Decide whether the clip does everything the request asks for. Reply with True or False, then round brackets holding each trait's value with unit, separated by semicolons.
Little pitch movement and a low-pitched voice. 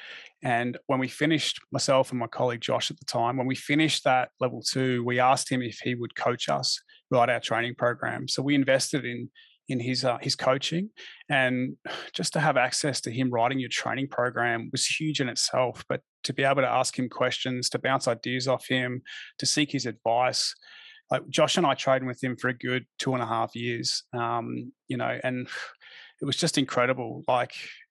True (2.1 semitones; 130 Hz)